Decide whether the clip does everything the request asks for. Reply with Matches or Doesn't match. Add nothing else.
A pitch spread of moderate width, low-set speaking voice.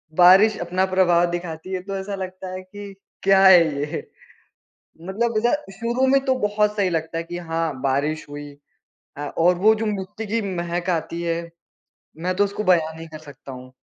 Doesn't match